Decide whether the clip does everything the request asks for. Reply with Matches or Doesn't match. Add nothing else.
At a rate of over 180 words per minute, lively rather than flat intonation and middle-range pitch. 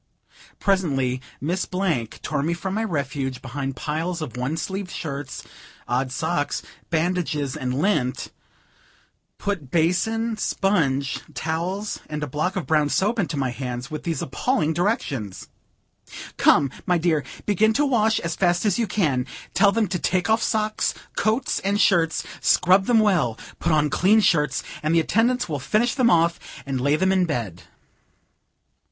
Doesn't match